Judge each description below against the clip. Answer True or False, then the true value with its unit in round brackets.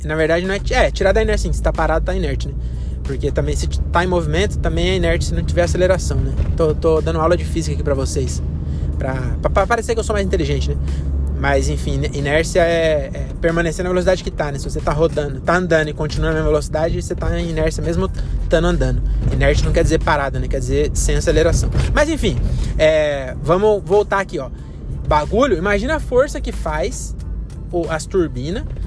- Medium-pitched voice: True (145 Hz)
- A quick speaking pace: True (210 wpm)